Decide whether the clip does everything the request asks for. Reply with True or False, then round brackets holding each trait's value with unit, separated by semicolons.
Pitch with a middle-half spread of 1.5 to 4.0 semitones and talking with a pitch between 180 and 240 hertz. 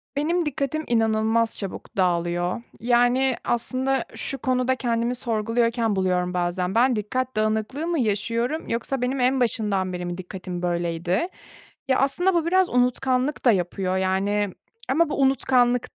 False (5.4 semitones; 235 Hz)